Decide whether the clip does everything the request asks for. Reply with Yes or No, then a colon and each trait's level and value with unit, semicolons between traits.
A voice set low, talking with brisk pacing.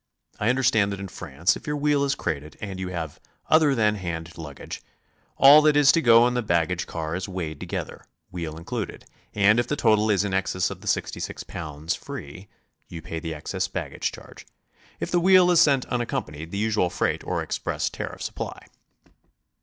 No: low, 100 Hz; average, 195 wpm